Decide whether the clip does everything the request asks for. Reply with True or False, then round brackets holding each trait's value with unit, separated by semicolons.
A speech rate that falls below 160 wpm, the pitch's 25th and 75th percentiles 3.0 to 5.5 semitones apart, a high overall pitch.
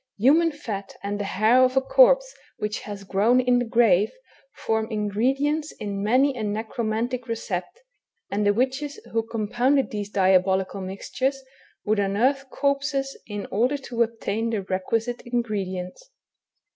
True (140 wpm; 4.4 semitones; 225 Hz)